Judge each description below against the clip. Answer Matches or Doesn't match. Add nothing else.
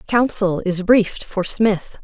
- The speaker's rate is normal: Matches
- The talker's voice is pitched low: Doesn't match